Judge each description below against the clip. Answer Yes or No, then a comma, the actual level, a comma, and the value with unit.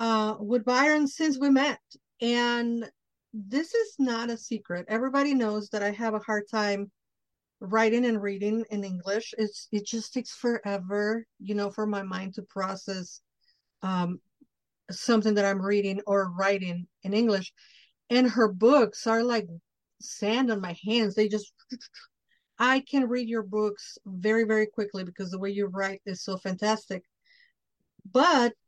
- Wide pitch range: No, average, 3.0 semitones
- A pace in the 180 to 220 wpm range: No, average, 155 wpm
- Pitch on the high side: Yes, high, 215 Hz